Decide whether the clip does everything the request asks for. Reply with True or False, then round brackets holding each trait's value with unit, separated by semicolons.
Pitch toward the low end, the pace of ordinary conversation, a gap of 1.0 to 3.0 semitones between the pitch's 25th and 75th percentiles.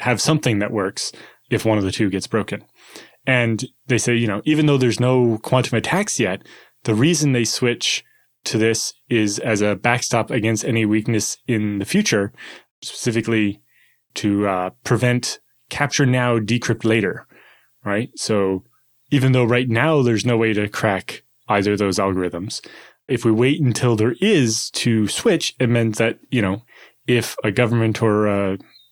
True (115 Hz; 165 wpm; 2.7 semitones)